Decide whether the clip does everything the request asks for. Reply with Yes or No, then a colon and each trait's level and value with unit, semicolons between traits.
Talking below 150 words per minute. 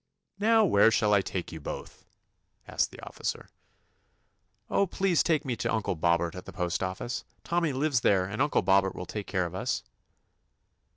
No: average, 175 wpm